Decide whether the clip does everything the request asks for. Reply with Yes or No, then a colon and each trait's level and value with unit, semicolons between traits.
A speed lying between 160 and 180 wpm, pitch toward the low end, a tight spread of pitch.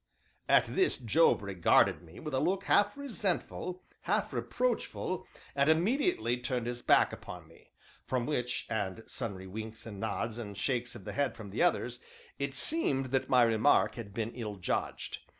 No: average, 170 wpm; low, 125 Hz; wide, 5.6 semitones